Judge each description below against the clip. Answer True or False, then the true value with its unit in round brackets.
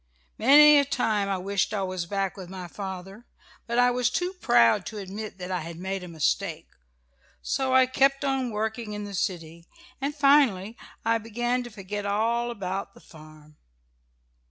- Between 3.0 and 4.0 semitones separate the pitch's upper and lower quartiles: False (4.8 semitones)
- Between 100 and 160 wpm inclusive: False (175 wpm)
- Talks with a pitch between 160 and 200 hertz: False (210 Hz)